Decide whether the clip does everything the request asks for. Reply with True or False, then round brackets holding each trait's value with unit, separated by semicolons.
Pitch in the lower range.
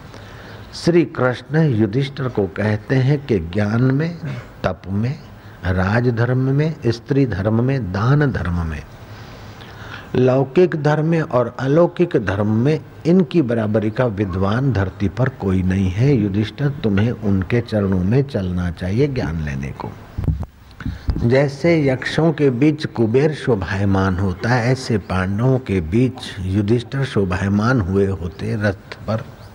True (115 Hz)